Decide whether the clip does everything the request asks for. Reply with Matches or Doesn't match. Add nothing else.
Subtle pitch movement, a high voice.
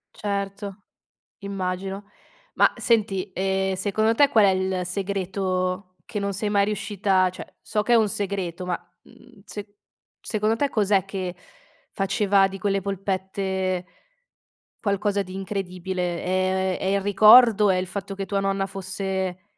Matches